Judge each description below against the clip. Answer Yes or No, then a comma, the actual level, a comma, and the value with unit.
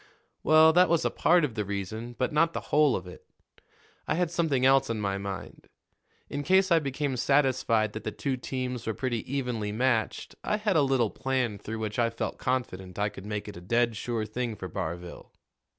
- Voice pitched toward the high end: No, low, 120 Hz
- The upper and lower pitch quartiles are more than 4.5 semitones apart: Yes, average, 4.9 semitones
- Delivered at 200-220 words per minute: Yes, fast, 205 wpm